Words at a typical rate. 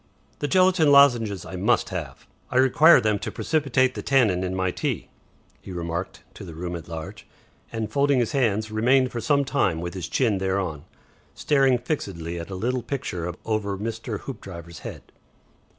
Yes: average, 170 wpm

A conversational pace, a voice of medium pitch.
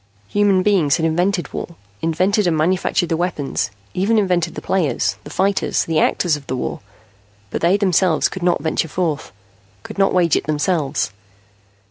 Yes: average, 165 wpm; medium, 175 Hz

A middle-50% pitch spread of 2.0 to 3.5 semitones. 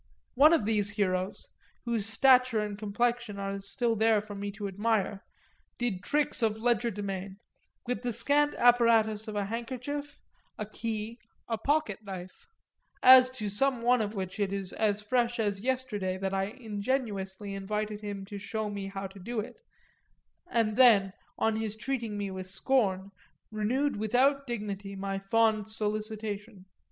Yes: average, 3.1 semitones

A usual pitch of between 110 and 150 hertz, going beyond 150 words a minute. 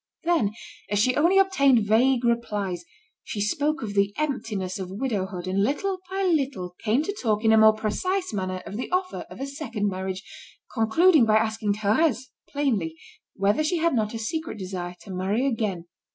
No: high, 220 Hz; average, 180 wpm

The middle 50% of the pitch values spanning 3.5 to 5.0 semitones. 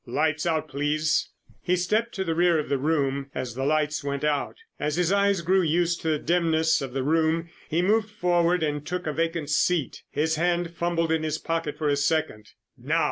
No: average, 2.7 semitones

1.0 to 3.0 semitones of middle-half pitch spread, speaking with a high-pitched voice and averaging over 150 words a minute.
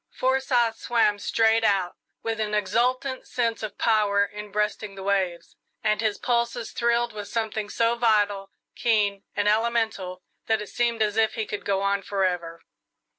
Yes: narrow, 2.5 semitones; high, 215 Hz; average, 160 wpm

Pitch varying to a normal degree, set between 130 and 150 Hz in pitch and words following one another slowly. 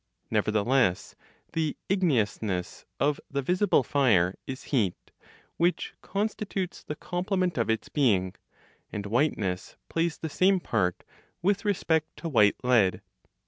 No: wide, 9.0 semitones; medium, 140 Hz; slow, 120 wpm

